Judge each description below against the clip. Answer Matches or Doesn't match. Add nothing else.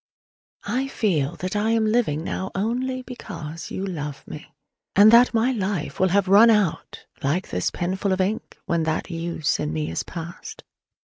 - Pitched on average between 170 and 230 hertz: Matches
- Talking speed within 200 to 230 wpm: Doesn't match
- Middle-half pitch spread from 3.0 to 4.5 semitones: Doesn't match